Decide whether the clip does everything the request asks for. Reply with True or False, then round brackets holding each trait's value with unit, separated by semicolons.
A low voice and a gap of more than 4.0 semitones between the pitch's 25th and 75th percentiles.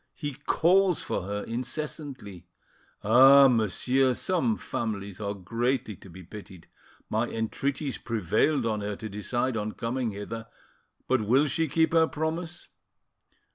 True (120 Hz; 5.4 semitones)